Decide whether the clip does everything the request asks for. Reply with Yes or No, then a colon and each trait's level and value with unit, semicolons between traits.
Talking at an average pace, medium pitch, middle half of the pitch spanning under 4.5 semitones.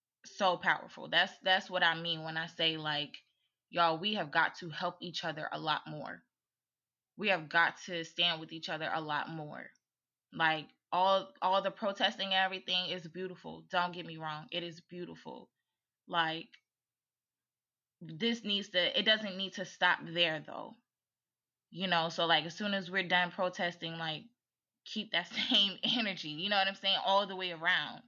Yes: average, 180 wpm; medium, 175 Hz; average, 2.8 semitones